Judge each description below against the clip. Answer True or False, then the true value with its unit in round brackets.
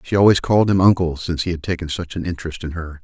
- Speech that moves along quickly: True (275 wpm)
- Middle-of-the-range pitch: False (85 Hz)